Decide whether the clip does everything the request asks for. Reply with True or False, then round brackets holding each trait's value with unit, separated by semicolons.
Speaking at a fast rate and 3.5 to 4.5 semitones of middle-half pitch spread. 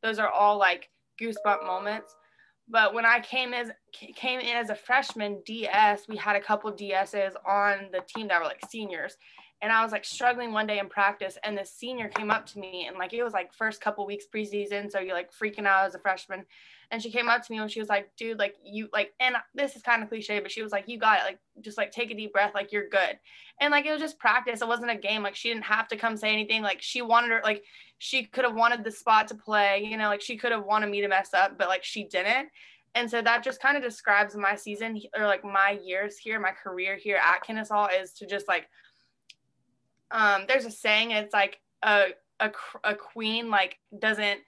False (245 wpm; 2.5 semitones)